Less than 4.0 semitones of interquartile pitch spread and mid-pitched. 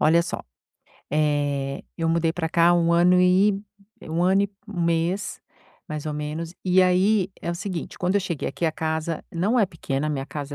Yes: average, 2.9 semitones; medium, 170 Hz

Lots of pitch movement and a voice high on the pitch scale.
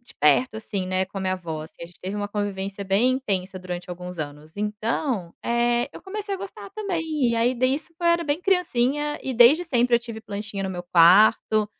Yes: wide, 5.8 semitones; high, 215 Hz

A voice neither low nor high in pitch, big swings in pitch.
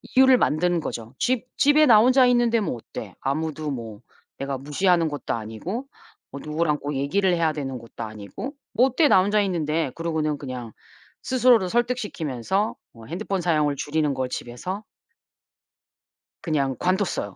Yes: medium, 160 Hz; wide, 7.4 semitones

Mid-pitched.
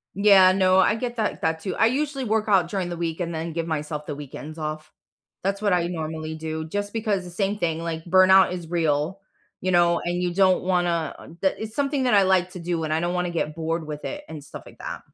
Yes: medium, 175 Hz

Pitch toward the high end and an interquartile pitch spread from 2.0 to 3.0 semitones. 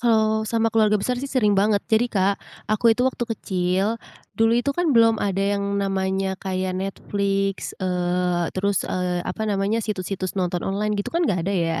Yes: high, 200 Hz; average, 2.7 semitones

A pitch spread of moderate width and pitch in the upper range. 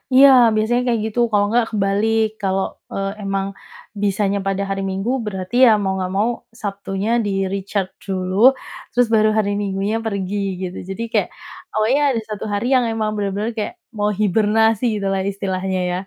No: narrow, 2.1 semitones; high, 200 Hz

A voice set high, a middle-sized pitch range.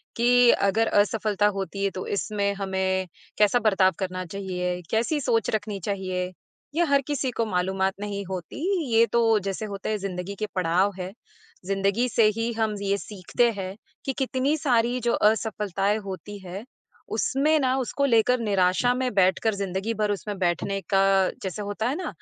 Yes: high, 205 Hz; average, 3.1 semitones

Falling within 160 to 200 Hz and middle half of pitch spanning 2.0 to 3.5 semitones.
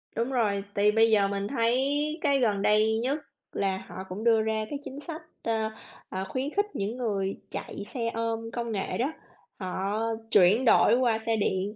No: high, 220 Hz; average, 2.9 semitones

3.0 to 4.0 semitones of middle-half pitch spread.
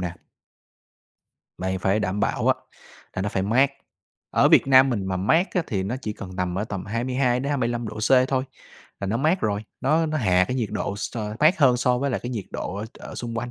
No: average, 4.8 semitones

